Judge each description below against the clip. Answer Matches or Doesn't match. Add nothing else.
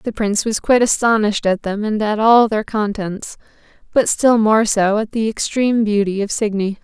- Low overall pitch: Doesn't match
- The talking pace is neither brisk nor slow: Matches